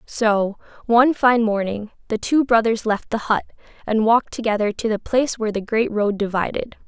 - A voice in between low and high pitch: No, high, 220 Hz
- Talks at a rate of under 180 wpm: No, average, 185 wpm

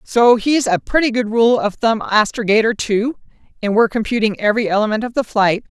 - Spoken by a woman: Yes, female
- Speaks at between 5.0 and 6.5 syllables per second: Yes, 5.7 syllables/s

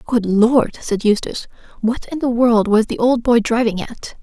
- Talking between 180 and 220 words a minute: Yes, average, 200 wpm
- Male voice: No, female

